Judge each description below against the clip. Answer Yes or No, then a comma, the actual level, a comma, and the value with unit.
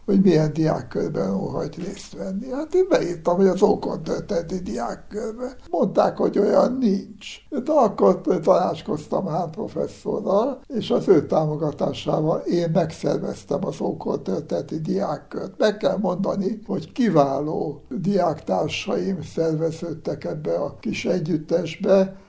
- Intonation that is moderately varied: Yes, average, 4.4 semitones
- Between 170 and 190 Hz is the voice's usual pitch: Yes, medium, 185 Hz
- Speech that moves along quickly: No, average, 115 wpm